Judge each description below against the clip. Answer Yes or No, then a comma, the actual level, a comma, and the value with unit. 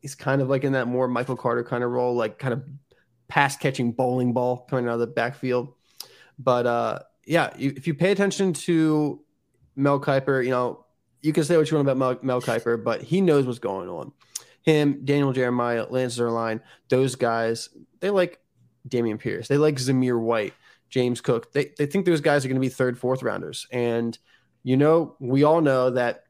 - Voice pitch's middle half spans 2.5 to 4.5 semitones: Yes, average, 2.8 semitones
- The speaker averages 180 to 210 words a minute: Yes, fast, 205 wpm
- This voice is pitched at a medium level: No, low, 130 Hz